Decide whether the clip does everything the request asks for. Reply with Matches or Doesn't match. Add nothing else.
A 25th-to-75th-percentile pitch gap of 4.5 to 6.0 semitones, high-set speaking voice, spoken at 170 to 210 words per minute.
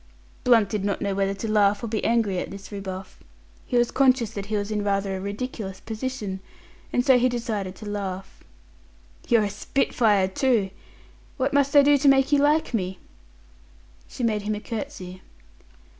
Doesn't match